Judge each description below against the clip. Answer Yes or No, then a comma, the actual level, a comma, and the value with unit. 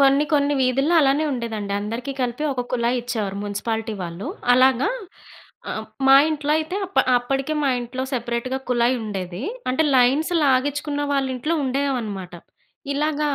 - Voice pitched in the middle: No, very high, 255 Hz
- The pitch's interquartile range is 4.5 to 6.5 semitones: No, average, 3.3 semitones